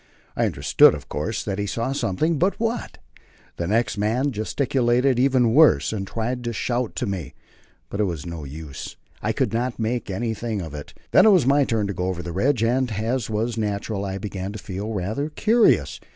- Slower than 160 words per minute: No, average, 200 wpm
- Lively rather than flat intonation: No, average, 4.6 semitones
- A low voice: Yes, low, 110 Hz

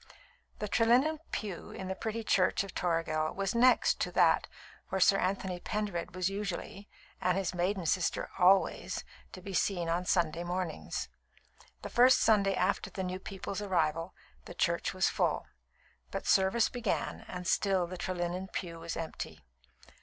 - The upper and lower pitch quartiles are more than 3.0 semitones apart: No, narrow, 2.4 semitones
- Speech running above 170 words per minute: No, average, 155 wpm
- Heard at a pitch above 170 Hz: Yes, medium, 185 Hz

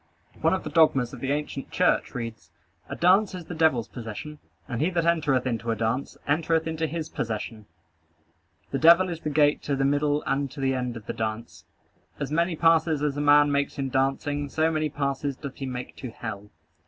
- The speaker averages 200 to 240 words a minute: Yes, fast, 205 wpm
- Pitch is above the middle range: No, medium, 145 Hz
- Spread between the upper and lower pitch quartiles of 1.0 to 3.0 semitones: No, average, 3.9 semitones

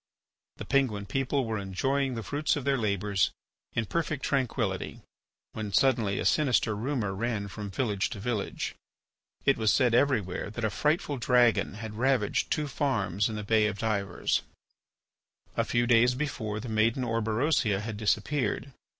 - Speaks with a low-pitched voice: Yes, low, 115 Hz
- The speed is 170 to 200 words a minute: No, average, 155 wpm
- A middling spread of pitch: Yes, average, 4.2 semitones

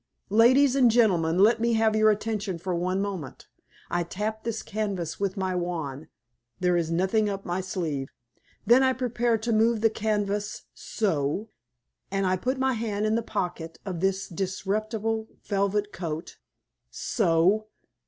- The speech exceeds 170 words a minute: No, average, 155 wpm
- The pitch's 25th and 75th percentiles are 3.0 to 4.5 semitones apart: Yes, average, 3.6 semitones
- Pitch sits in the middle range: No, high, 205 Hz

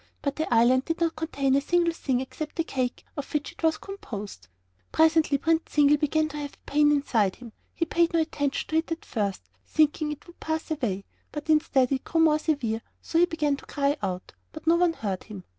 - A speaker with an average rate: No, fast, 225 wpm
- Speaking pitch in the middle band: No, very high, 295 Hz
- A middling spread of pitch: Yes, average, 3.8 semitones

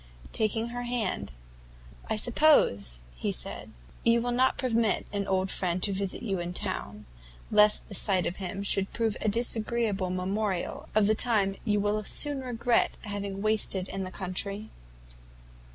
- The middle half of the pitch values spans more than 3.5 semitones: No, average, 3.2 semitones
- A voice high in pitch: Yes, high, 205 Hz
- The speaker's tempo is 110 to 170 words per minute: Yes, average, 155 wpm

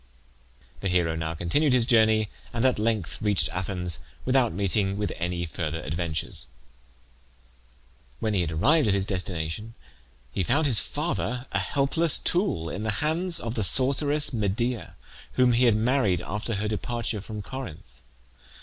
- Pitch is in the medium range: No, low, 110 Hz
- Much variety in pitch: Yes, wide, 6.0 semitones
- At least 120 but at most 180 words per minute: Yes, average, 150 wpm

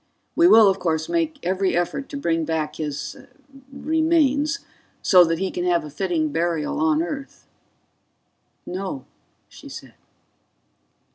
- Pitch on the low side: No, medium, 185 Hz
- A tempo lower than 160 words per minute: Yes, slow, 135 wpm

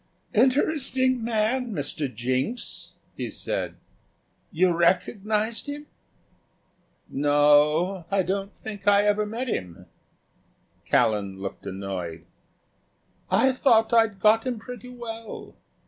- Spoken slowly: Yes, slow, 110 wpm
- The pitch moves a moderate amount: No, wide, 8.1 semitones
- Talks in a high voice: Yes, high, 205 Hz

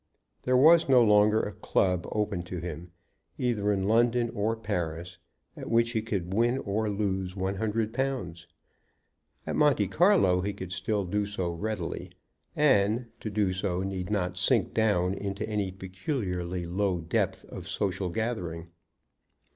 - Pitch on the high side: No, low, 100 Hz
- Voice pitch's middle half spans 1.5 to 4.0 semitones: Yes, average, 3.4 semitones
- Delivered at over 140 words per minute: Yes, average, 150 wpm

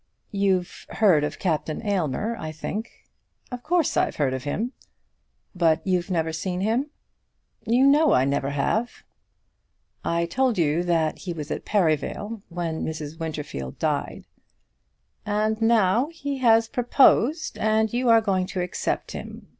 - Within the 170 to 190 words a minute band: No, average, 145 wpm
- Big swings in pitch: Yes, wide, 6.2 semitones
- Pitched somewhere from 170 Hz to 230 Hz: Yes, high, 190 Hz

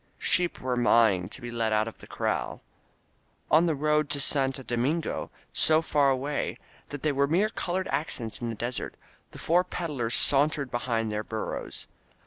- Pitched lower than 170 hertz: Yes, low, 135 Hz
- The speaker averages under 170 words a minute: No, average, 175 wpm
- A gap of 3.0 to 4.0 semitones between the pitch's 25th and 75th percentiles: No, average, 4.5 semitones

